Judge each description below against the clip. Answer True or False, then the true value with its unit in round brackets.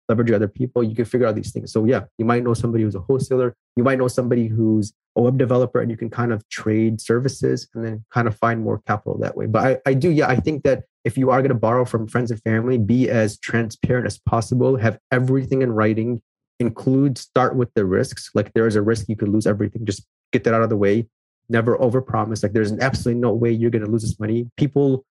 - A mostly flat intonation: True (2.3 semitones)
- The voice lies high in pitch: False (115 Hz)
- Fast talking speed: True (250 wpm)